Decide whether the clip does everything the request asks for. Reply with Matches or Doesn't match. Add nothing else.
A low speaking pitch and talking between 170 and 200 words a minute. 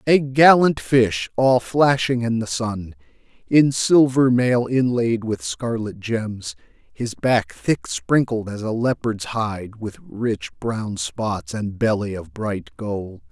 Doesn't match